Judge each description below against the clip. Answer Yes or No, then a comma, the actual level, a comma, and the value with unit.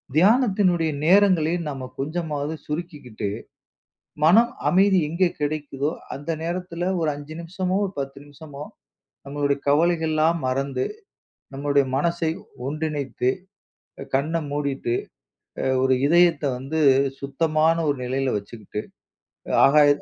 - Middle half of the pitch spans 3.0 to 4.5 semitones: Yes, average, 3.4 semitones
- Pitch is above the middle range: No, medium, 155 Hz